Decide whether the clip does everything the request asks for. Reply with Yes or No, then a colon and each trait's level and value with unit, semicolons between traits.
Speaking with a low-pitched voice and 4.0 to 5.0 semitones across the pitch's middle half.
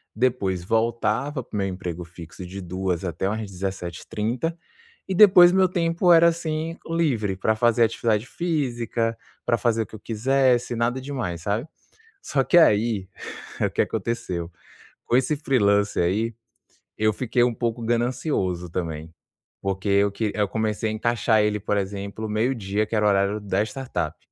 Yes: low, 110 Hz; average, 4.3 semitones